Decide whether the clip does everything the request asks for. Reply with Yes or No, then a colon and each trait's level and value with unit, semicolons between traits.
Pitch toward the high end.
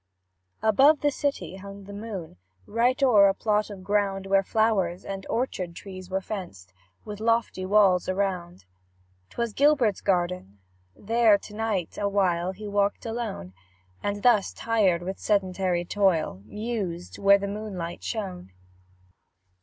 Yes: high, 200 Hz